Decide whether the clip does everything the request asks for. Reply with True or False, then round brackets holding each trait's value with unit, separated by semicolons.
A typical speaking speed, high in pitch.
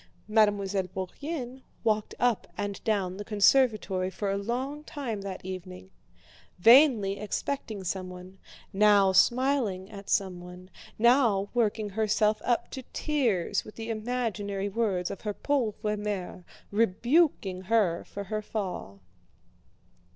False (120 wpm; 210 Hz)